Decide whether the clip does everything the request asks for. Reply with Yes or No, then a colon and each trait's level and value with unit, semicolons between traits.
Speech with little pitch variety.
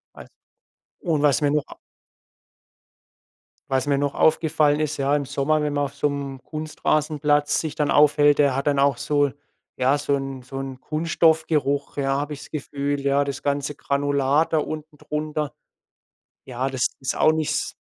Yes: narrow, 1.5 semitones